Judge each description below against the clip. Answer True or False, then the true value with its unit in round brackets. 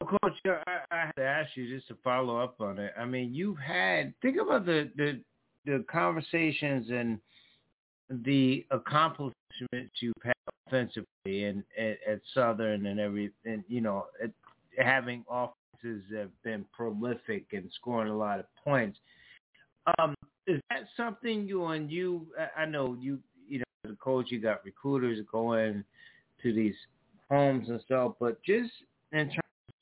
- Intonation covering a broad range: False (4.8 semitones)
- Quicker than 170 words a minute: False (155 wpm)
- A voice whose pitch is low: True (125 Hz)